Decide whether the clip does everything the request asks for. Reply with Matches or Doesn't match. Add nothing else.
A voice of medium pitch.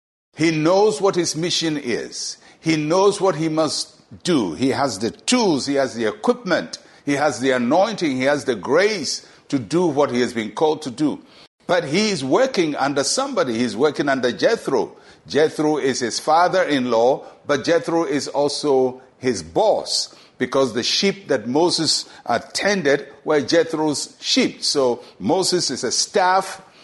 Matches